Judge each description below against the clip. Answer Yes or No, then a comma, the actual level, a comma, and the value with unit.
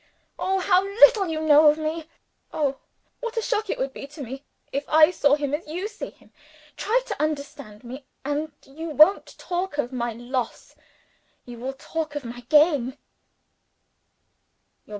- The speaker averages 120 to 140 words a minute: No, average, 165 wpm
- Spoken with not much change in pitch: No, average, 4.1 semitones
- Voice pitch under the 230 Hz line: No, very high, 300 Hz